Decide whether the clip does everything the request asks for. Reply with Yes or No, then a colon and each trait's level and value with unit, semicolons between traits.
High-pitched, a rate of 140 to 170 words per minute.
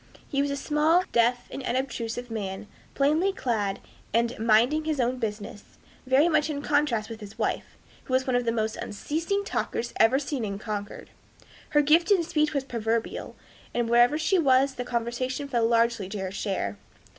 No: high, 245 Hz; average, 180 wpm